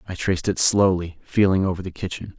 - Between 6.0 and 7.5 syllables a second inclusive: Yes, 6.1 syllables/s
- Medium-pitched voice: No, very low, 95 Hz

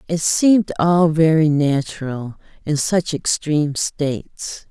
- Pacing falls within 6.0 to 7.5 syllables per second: No, 3.8 syllables/s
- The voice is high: No, medium, 155 Hz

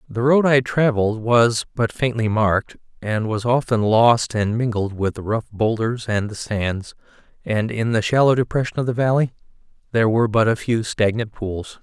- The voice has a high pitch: No, low, 115 Hz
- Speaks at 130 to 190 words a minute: Yes, average, 185 wpm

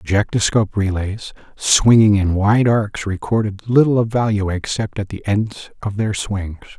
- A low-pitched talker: Yes, low, 105 Hz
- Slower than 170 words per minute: Yes, average, 160 wpm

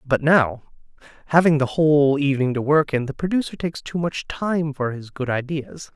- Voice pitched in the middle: Yes, medium, 145 Hz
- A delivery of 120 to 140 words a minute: No, average, 190 wpm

